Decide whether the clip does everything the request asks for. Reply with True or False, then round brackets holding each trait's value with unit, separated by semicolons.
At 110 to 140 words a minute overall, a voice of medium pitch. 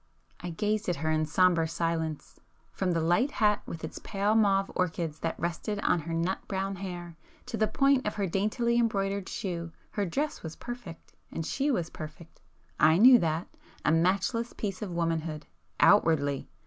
False (165 wpm; 180 Hz)